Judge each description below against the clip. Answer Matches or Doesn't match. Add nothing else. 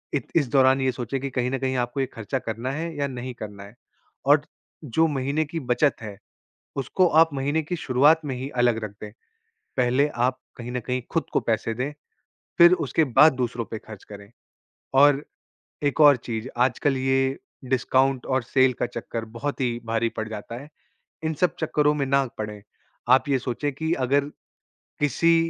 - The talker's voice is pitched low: Matches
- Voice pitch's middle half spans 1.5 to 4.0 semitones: Matches